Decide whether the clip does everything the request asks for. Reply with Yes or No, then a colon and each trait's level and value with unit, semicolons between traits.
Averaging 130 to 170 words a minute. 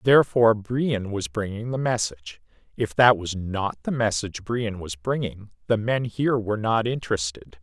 Yes: average, 165 wpm